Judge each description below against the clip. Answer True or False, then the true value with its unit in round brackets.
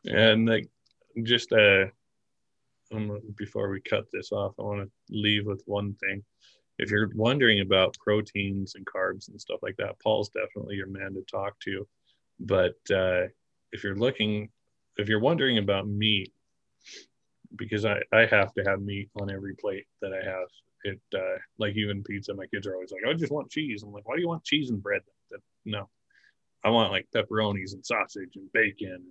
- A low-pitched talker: True (105 Hz)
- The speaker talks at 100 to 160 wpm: False (190 wpm)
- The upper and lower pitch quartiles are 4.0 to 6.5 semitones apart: False (2.8 semitones)